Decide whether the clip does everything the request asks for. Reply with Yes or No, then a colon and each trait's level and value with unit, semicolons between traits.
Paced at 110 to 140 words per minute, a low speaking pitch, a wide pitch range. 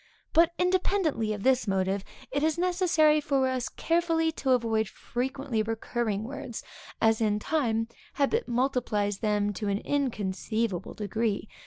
No: slow, 135 wpm; high, 240 Hz; wide, 5.9 semitones